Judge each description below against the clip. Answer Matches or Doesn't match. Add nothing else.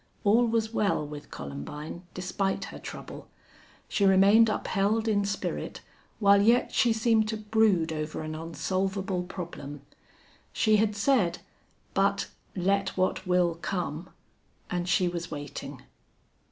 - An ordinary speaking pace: Doesn't match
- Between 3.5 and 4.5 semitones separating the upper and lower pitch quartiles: Matches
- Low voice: Doesn't match